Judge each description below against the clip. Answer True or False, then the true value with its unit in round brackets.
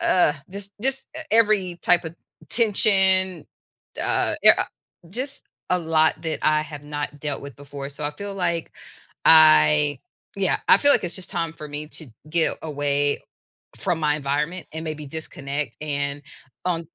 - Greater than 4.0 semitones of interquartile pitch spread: False (3.7 semitones)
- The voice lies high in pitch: False (160 Hz)